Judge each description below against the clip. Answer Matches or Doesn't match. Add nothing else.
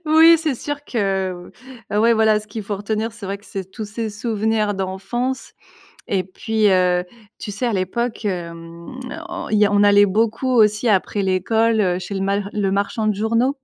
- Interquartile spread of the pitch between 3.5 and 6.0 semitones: Doesn't match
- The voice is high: Matches